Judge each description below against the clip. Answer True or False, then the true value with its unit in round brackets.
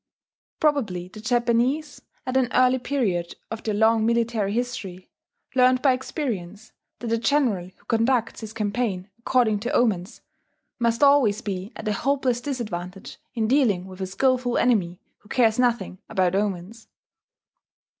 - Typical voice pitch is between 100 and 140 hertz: False (230 Hz)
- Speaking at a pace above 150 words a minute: False (145 wpm)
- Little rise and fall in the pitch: False (4.2 semitones)